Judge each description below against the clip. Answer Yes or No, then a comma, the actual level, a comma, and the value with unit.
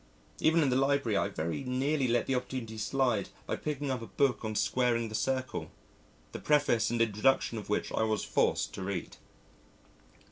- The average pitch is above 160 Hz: No, low, 125 Hz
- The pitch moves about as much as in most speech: Yes, average, 3.5 semitones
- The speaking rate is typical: Yes, average, 185 wpm